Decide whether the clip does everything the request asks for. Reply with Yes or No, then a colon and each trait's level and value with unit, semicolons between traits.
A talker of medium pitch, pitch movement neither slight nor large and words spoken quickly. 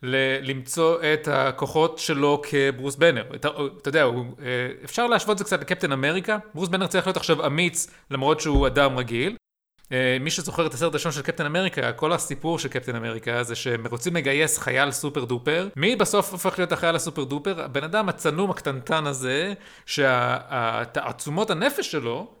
Yes: medium, 150 Hz; average, 4.6 semitones; fast, 170 wpm